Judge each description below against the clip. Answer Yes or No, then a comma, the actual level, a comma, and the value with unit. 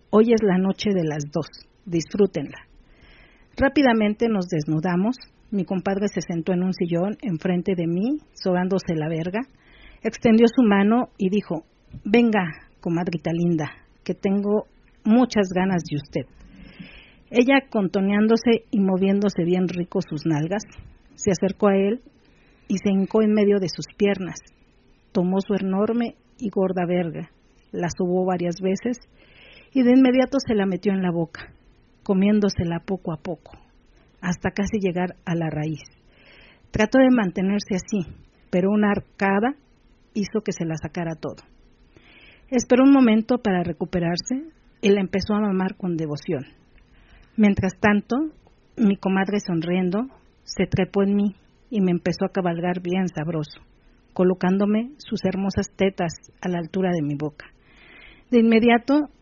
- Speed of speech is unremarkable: Yes, average, 140 wpm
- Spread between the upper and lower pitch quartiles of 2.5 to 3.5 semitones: Yes, average, 3.2 semitones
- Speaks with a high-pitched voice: Yes, high, 195 Hz